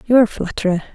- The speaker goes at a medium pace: No, fast, 255 wpm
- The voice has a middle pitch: No, high, 210 Hz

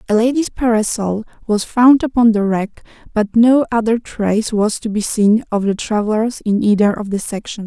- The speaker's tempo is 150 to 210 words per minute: Yes, average, 190 wpm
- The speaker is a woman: Yes, female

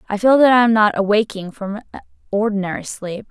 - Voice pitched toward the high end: Yes, high, 210 Hz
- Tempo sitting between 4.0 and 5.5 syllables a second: No, 5.8 syllables/s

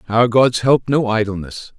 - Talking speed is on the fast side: No, average, 170 wpm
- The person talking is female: No, male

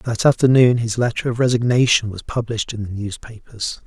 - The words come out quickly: No, average, 170 wpm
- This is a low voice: Yes, low, 115 Hz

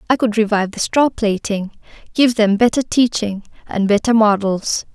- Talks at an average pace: Yes, average, 160 wpm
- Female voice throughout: Yes, female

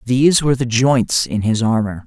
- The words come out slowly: No, fast, 205 wpm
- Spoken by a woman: No, male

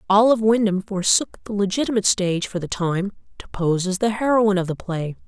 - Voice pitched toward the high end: Yes, high, 200 Hz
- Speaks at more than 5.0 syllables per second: Yes, 6.0 syllables/s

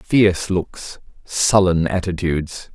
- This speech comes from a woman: No, male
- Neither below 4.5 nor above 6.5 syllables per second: No, 3.7 syllables/s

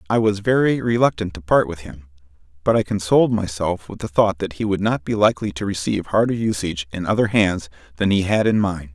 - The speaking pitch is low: Yes, low, 100 Hz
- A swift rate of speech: Yes, fast, 220 wpm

